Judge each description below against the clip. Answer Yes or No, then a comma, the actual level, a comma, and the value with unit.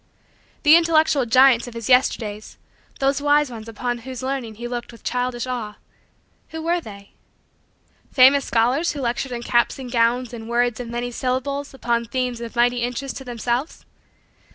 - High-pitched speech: Yes, high, 245 Hz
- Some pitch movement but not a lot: No, narrow, 2.2 semitones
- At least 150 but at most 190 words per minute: Yes, average, 165 wpm